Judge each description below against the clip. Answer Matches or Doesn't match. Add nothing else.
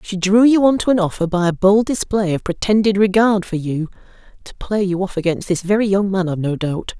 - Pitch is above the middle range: Matches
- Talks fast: Matches